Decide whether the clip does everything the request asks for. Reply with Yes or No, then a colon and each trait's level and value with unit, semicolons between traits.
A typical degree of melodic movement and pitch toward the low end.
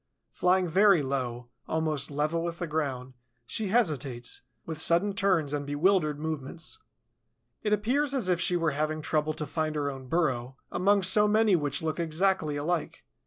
No: average, 4.3 semitones; medium, 160 Hz